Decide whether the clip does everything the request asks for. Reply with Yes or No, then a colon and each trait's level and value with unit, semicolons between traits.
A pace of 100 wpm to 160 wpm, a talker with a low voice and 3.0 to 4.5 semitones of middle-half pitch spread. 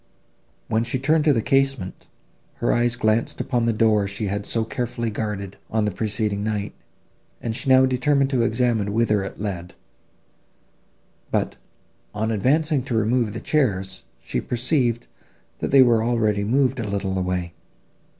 Yes: average, 155 wpm; low, 115 Hz; average, 3.5 semitones